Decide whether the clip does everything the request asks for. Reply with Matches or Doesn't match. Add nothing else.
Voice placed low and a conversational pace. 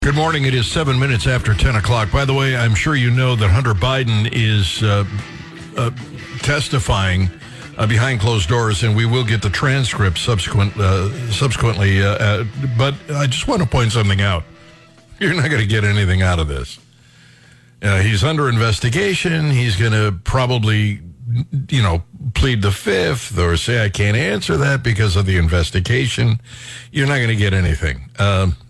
Matches